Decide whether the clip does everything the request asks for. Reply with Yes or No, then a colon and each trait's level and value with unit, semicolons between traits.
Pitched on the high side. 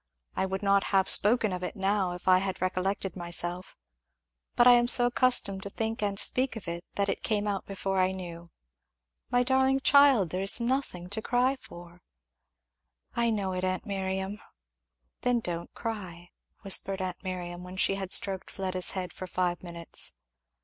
Yes: high, 195 Hz